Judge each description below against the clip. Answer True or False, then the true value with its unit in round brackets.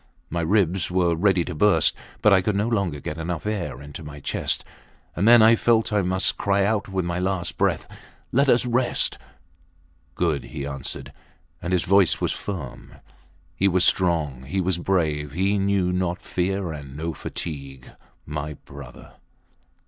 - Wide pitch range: False (4.3 semitones)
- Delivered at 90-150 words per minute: False (165 wpm)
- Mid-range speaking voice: False (90 Hz)